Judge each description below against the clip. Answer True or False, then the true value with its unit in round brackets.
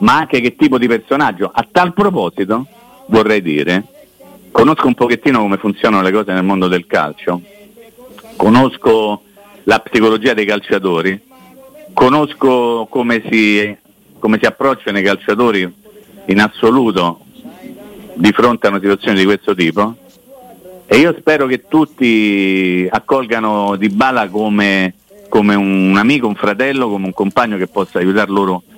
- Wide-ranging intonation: True (7.6 semitones)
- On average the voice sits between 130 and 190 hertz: False (110 Hz)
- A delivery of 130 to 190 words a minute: True (135 wpm)